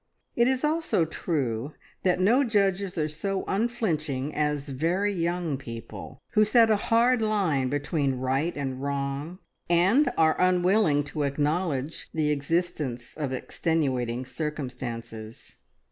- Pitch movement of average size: No, wide, 5.8 semitones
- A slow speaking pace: Yes, slow, 125 wpm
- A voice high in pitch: No, medium, 155 Hz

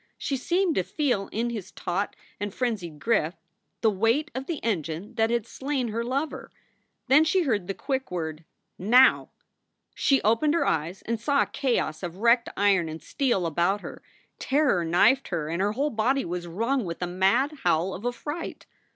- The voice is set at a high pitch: Yes, high, 225 Hz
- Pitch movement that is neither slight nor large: No, wide, 6.9 semitones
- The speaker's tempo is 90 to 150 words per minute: No, average, 180 wpm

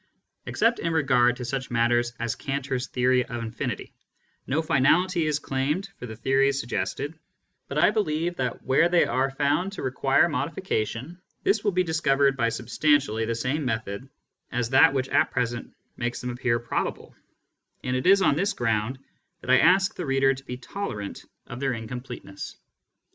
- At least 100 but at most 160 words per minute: No, average, 170 wpm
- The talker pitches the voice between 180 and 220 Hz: No, low, 135 Hz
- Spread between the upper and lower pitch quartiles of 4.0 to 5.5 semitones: Yes, average, 4.4 semitones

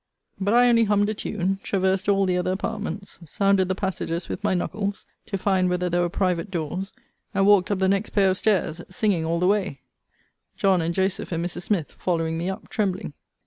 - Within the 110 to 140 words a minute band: No, fast, 205 wpm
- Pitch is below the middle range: No, high, 190 Hz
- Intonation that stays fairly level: Yes, narrow, 2.2 semitones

